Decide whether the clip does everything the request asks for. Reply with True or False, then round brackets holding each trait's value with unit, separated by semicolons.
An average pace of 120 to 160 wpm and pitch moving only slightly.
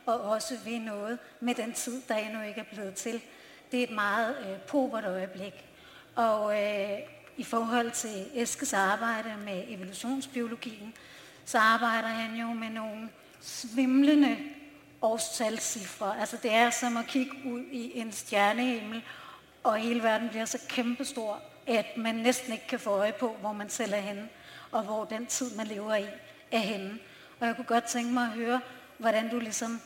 False (175 wpm; 2.2 semitones)